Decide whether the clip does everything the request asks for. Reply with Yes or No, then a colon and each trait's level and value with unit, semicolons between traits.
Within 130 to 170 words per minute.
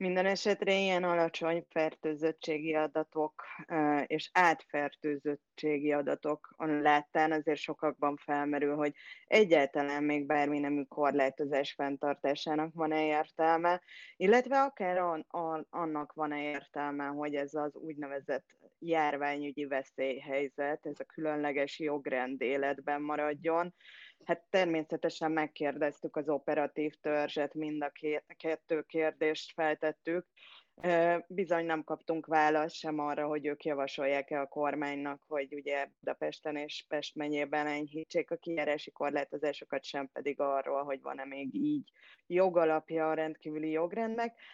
No: average, 115 wpm